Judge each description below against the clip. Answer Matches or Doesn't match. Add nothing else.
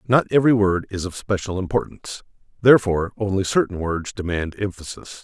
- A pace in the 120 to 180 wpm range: Matches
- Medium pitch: Doesn't match